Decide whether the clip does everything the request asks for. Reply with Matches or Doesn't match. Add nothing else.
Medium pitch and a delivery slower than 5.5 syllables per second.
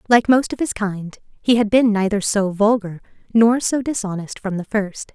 Doesn't match